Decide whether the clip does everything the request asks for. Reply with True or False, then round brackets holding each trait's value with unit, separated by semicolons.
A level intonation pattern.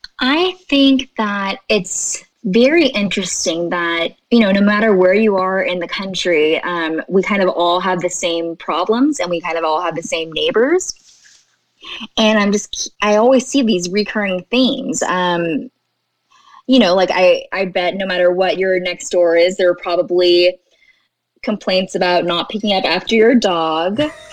False (4.4 semitones)